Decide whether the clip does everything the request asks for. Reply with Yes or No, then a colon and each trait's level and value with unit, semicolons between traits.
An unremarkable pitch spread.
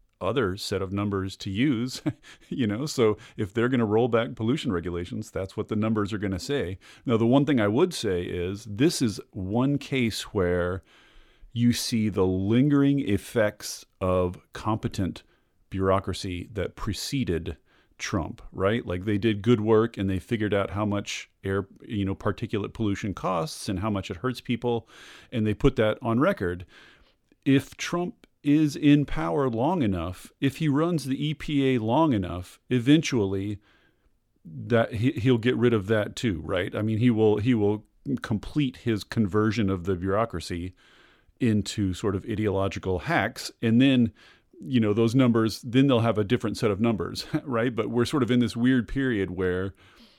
Yes: average, 4.1 semitones